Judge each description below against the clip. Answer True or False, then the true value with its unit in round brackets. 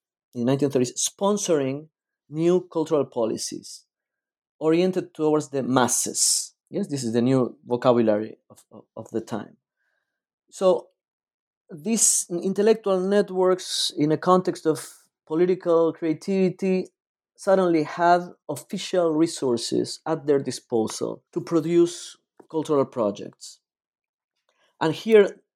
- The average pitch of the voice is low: False (160 Hz)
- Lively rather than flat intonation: False (5.0 semitones)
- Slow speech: True (105 wpm)